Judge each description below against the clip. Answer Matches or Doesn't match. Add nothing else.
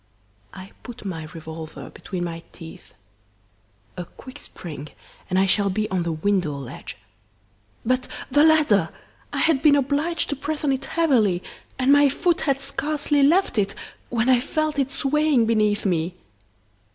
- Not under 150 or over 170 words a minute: Matches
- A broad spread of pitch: Matches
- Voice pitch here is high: Matches